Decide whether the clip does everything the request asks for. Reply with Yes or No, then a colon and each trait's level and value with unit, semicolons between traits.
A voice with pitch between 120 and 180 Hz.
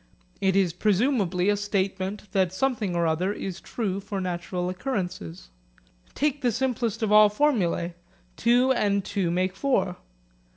No: high, 195 Hz